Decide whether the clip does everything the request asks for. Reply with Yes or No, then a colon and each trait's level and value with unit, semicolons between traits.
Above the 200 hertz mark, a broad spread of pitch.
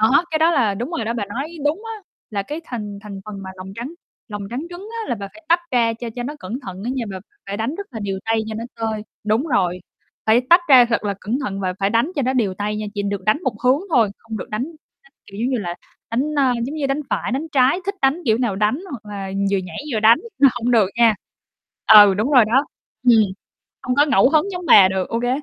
No: high, 230 Hz; average, 4.9 semitones